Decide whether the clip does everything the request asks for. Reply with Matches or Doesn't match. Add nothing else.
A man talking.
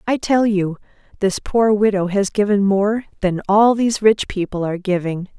Doesn't match